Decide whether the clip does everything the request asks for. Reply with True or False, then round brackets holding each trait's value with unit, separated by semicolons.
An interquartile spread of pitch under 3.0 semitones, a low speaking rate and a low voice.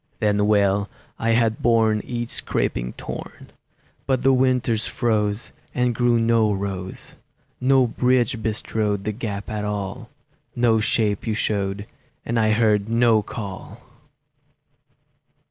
True (2.5 semitones; 125 wpm; 110 Hz)